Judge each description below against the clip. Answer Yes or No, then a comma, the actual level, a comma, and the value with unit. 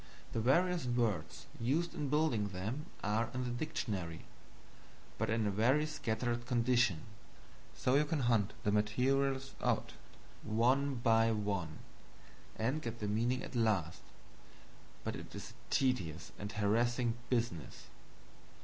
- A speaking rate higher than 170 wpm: No, slow, 135 wpm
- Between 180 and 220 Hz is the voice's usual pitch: No, low, 120 Hz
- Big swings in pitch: No, average, 3.9 semitones